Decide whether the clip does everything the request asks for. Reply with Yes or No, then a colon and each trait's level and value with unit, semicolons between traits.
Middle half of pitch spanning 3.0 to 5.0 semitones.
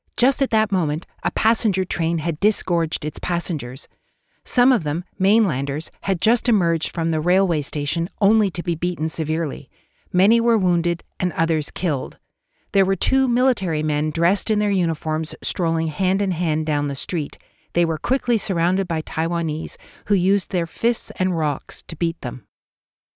Yes: average, 3.9 semitones